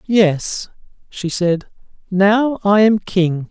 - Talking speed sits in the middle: No, slow, 120 wpm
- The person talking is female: No, male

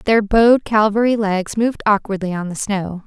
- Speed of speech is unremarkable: Yes, average, 175 wpm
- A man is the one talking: No, female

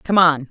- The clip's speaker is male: No, female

